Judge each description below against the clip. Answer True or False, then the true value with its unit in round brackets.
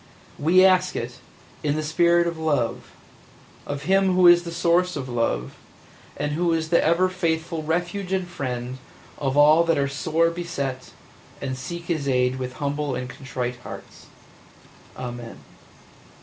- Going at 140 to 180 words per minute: True (150 wpm)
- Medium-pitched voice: True (155 Hz)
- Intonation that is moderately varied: True (4.7 semitones)